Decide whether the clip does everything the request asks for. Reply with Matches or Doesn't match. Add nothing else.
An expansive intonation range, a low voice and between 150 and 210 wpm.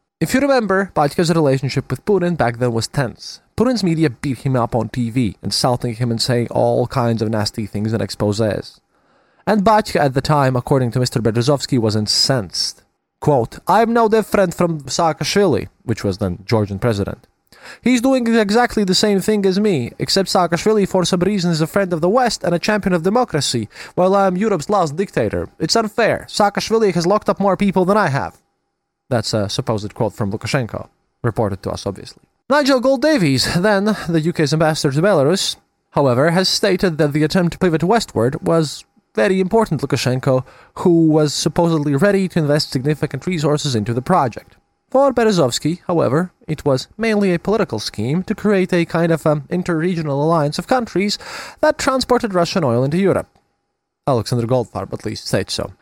Doesn't match